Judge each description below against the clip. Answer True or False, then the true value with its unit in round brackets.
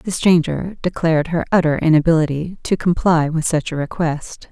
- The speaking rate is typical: True (160 wpm)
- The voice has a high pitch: False (165 Hz)